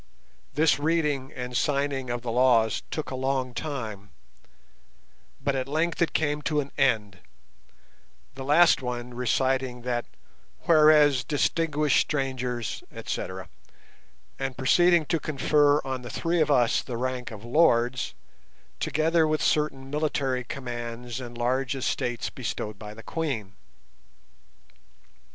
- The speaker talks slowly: Yes, slow, 125 wpm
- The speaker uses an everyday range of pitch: Yes, average, 3.5 semitones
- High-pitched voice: No, low, 130 Hz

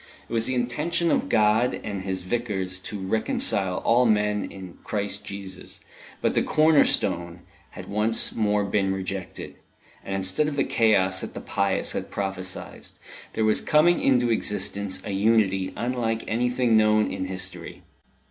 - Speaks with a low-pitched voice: Yes, low, 105 Hz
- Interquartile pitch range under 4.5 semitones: Yes, average, 3.4 semitones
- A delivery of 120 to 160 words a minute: Yes, average, 155 wpm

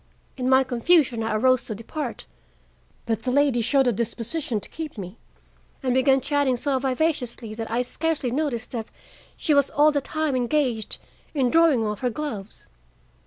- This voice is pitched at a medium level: No, very high, 255 Hz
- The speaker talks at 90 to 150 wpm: No, average, 165 wpm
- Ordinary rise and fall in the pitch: Yes, average, 3.9 semitones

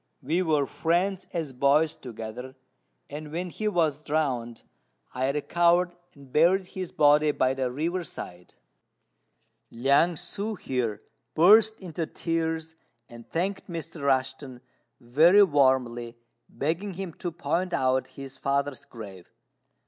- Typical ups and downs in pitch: Yes, average, 4.8 semitones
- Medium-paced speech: No, slow, 125 wpm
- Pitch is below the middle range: No, medium, 150 Hz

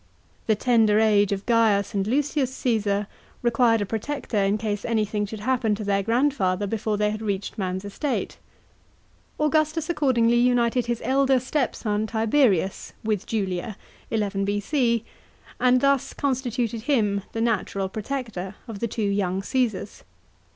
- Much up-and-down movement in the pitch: No, average, 3.5 semitones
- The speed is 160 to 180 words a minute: No, average, 145 wpm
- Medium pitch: No, high, 220 Hz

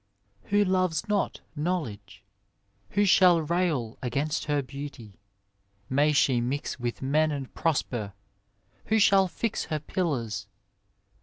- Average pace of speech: No, slow, 120 wpm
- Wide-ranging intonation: Yes, wide, 6.3 semitones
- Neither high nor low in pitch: Yes, medium, 150 Hz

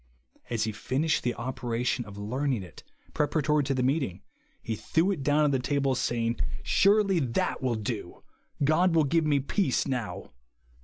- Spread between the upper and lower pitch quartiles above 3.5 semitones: Yes, average, 4.4 semitones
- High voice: No, low, 135 Hz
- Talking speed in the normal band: Yes, average, 165 wpm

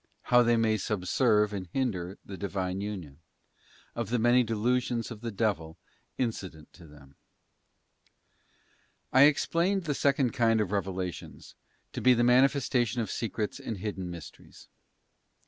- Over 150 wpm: No, average, 140 wpm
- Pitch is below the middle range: Yes, low, 110 Hz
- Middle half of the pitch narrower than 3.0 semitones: No, average, 4.6 semitones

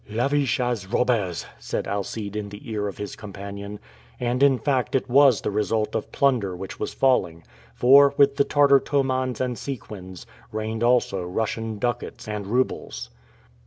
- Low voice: Yes, low, 115 Hz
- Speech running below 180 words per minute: Yes, average, 160 wpm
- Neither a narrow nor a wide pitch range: Yes, average, 4.2 semitones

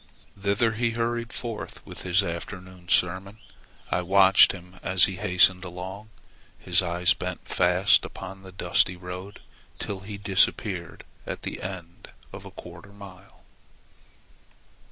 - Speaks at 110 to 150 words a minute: Yes, average, 140 wpm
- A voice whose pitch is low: Yes, very low, 95 Hz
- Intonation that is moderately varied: No, narrow, 1.9 semitones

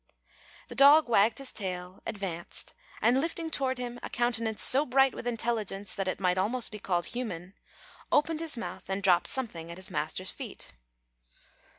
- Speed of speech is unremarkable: Yes, average, 170 wpm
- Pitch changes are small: No, wide, 5.4 semitones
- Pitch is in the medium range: No, high, 225 Hz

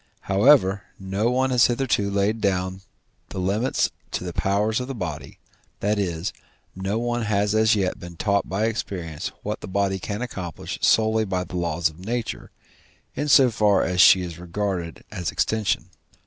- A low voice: Yes, low, 100 Hz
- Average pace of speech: Yes, average, 170 wpm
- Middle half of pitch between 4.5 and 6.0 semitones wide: No, average, 3.3 semitones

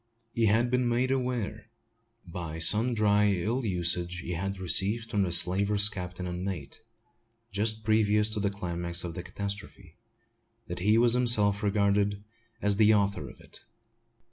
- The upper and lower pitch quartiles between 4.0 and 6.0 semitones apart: No, average, 3.4 semitones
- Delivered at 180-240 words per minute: No, average, 150 wpm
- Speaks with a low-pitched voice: Yes, low, 100 Hz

